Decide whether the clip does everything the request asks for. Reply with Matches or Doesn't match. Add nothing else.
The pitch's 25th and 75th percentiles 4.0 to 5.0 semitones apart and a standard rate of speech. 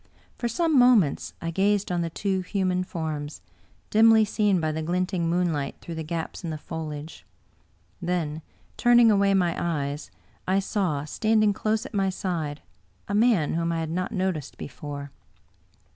Matches